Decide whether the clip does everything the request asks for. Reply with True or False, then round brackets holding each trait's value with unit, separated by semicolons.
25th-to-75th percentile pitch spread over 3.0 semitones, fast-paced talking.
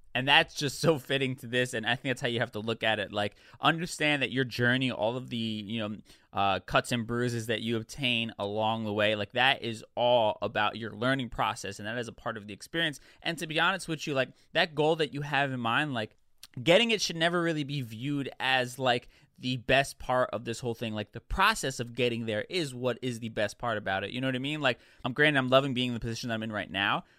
True (3.5 semitones; 260 wpm)